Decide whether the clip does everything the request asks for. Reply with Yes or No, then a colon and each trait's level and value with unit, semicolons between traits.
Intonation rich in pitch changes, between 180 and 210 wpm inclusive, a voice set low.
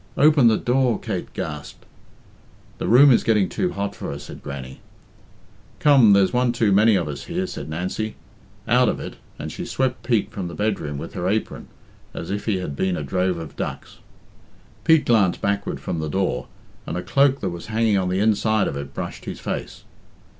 No: average, 4.8 semitones; average, 195 wpm; low, 100 Hz